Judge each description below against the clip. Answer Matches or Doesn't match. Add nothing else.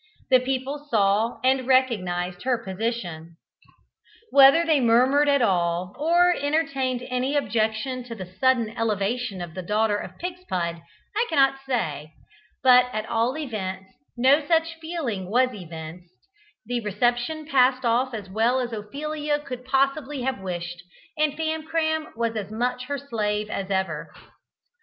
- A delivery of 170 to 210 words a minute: Doesn't match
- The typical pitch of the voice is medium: Doesn't match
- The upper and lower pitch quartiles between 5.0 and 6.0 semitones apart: Matches